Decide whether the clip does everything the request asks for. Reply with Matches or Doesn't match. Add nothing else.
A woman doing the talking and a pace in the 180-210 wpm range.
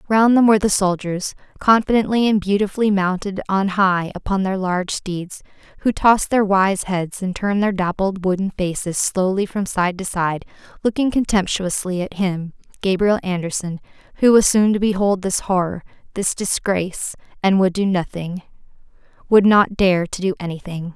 Doesn't match